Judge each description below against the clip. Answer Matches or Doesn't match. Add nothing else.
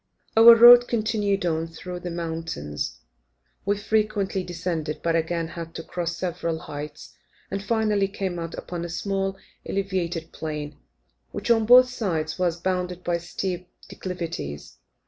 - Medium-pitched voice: Matches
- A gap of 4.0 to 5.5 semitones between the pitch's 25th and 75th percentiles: Doesn't match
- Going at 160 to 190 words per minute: Doesn't match